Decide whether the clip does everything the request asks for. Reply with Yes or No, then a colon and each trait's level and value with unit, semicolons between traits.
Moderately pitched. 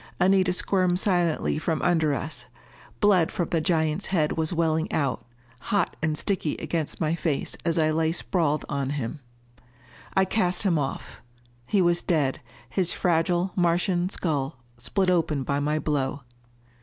Yes: medium, 165 Hz